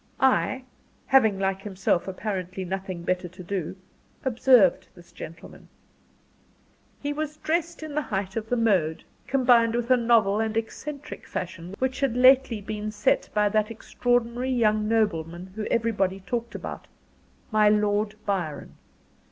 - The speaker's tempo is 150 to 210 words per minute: No, average, 140 wpm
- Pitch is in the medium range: No, high, 215 Hz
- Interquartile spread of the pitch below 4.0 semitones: No, average, 4.3 semitones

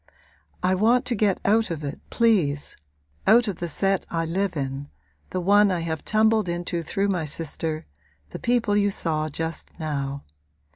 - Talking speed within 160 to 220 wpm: Yes, average, 165 wpm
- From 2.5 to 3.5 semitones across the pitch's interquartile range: No, average, 4.6 semitones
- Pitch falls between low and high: Yes, medium, 175 Hz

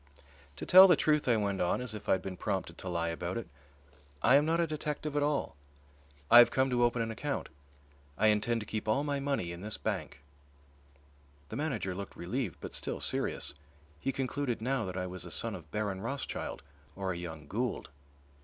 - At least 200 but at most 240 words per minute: Yes, fast, 205 wpm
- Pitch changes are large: Yes, wide, 6.6 semitones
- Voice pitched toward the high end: No, low, 115 Hz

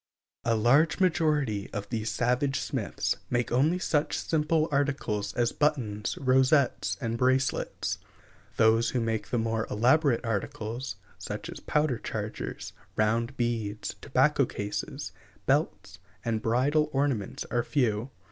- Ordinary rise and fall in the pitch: Yes, average, 4.3 semitones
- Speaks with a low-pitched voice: Yes, low, 125 Hz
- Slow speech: Yes, slow, 130 wpm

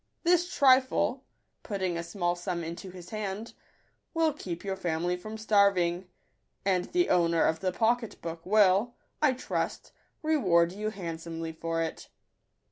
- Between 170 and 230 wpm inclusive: No, average, 150 wpm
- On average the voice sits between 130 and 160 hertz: No, high, 190 Hz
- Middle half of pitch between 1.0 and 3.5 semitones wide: No, average, 4.4 semitones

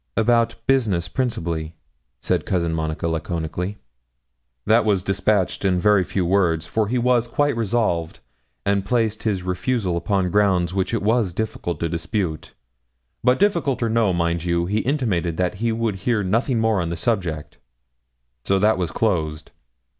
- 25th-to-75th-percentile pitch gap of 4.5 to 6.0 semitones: Yes, average, 4.9 semitones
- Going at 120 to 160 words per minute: Yes, average, 155 wpm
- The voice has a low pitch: Yes, low, 100 Hz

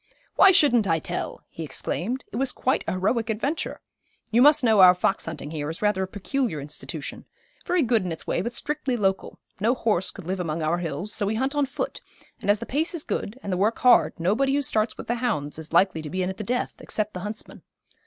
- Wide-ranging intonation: Yes, wide, 5.7 semitones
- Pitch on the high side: Yes, high, 210 Hz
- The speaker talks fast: Yes, fast, 235 wpm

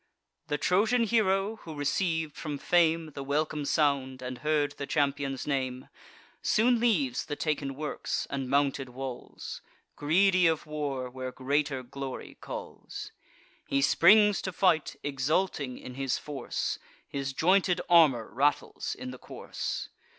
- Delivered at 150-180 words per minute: No, slow, 135 wpm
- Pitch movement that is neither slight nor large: Yes, average, 3.9 semitones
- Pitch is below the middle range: No, medium, 145 Hz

